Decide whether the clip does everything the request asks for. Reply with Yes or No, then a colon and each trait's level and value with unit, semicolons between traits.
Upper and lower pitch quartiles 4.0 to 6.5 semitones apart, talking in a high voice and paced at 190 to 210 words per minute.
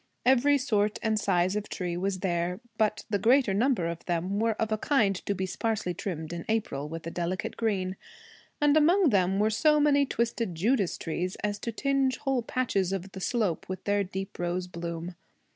Yes: average, 4.4 semitones; high, 200 Hz; average, 195 wpm